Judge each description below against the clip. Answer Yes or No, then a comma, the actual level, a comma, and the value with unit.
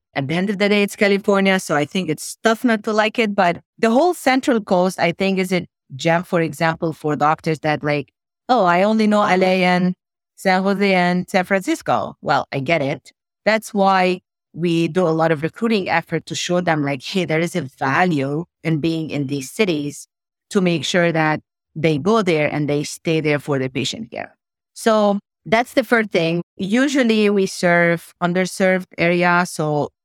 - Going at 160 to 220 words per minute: Yes, average, 195 wpm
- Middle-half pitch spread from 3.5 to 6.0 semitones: Yes, average, 4.1 semitones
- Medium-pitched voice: Yes, medium, 180 Hz